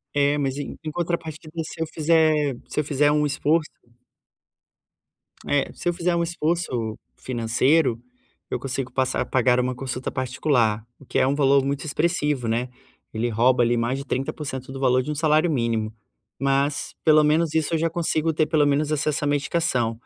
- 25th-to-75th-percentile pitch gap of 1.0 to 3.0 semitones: No, average, 3.4 semitones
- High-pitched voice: No, medium, 145 Hz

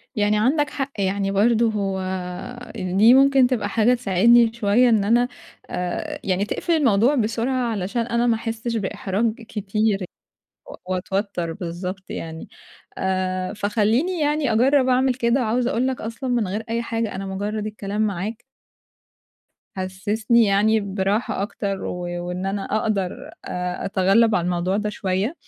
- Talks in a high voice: Yes, high, 215 Hz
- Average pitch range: Yes, average, 3.4 semitones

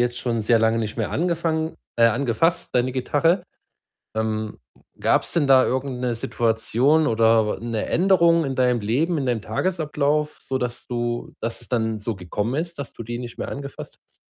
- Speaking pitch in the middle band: No, low, 125 Hz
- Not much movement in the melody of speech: No, average, 4.7 semitones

